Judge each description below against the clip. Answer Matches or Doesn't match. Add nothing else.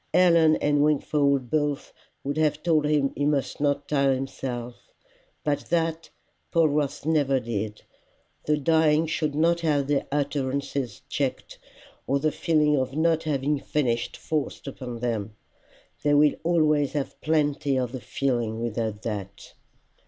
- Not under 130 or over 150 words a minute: Matches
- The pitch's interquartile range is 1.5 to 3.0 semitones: Matches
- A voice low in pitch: Doesn't match